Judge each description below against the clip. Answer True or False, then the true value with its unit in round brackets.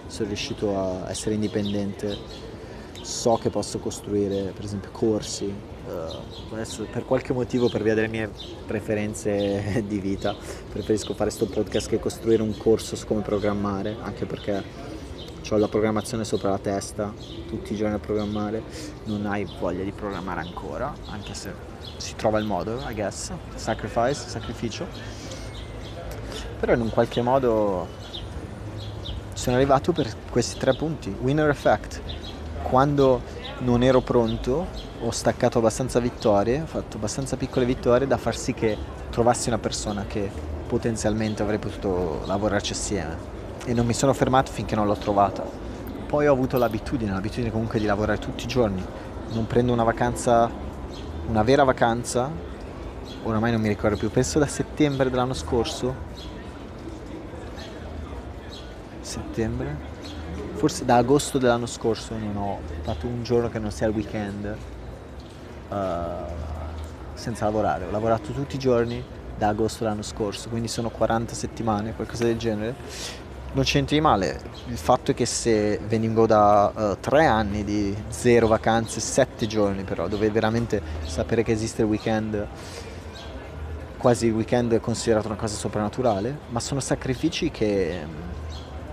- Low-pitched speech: True (110 Hz)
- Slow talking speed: False (145 wpm)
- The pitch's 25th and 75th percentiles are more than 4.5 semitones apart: False (2.7 semitones)